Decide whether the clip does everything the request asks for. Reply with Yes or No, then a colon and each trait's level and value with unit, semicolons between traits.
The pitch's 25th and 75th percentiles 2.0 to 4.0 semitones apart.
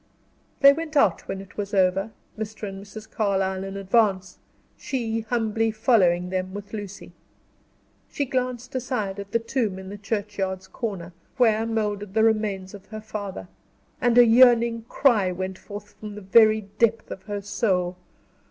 Yes: average, 2.8 semitones